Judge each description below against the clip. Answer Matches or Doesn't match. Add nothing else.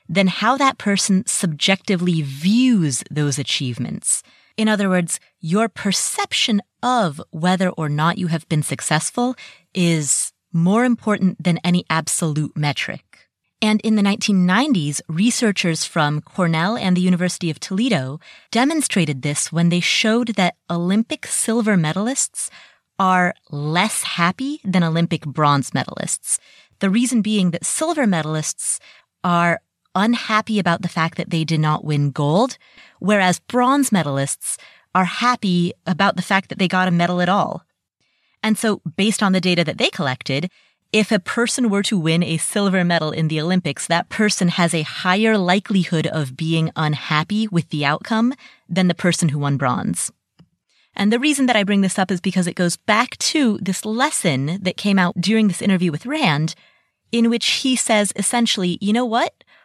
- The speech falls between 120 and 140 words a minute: Doesn't match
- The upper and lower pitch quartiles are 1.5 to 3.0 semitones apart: Doesn't match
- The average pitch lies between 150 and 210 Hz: Matches